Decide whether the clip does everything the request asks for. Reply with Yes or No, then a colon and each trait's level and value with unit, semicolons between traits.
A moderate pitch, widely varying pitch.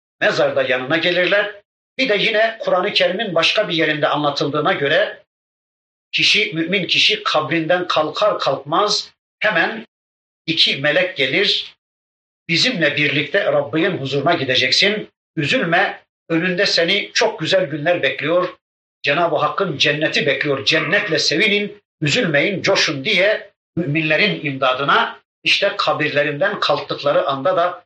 No: medium, 165 Hz; average, 4.9 semitones